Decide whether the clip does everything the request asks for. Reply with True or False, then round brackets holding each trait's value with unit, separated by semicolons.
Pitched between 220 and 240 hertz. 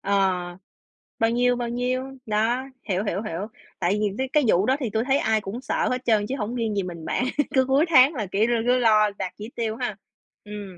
True (225 Hz)